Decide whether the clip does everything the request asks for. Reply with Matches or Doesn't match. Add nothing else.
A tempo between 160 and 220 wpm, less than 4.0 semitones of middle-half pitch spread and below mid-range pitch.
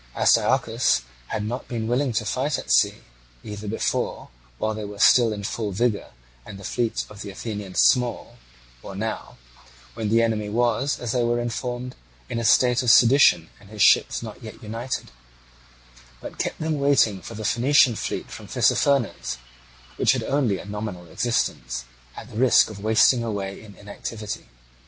Matches